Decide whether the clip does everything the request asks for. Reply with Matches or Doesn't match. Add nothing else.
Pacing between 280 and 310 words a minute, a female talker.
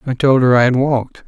Doesn't match